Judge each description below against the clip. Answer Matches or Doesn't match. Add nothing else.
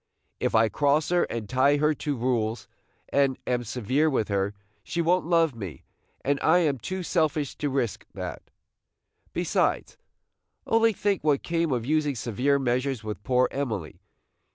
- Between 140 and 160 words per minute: Matches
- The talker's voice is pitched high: Doesn't match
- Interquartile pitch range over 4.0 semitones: Matches